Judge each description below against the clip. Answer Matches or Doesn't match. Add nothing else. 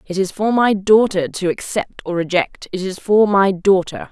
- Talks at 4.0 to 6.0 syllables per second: Matches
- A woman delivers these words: Matches